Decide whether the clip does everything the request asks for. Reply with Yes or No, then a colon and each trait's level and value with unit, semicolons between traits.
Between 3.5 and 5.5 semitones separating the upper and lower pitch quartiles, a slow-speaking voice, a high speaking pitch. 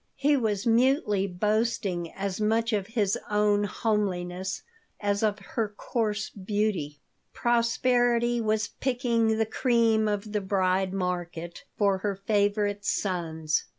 No: average, 2.8 semitones; slow, 120 wpm; high, 210 Hz